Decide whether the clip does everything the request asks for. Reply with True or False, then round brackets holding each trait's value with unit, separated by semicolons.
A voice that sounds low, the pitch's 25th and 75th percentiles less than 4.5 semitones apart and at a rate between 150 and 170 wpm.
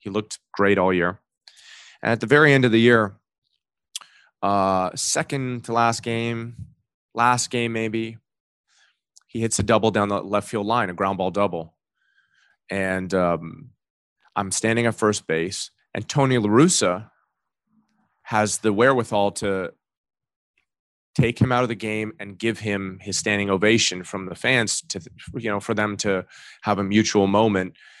True (105 Hz; 2.8 semitones; 155 wpm)